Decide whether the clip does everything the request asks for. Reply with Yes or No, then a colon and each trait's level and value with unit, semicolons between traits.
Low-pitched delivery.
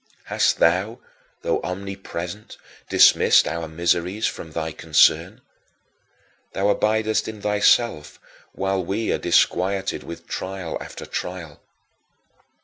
Yes: very low, 95 Hz